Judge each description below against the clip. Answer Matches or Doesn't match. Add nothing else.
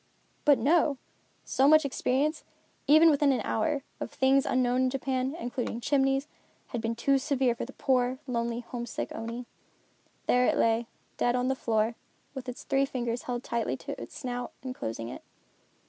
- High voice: Matches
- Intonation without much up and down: Matches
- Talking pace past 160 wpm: Matches